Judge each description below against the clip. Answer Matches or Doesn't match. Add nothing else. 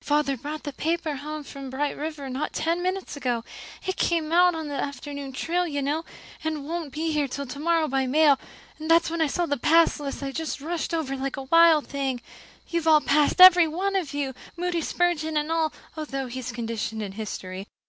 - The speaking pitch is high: Matches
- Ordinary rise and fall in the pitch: Matches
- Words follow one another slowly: Doesn't match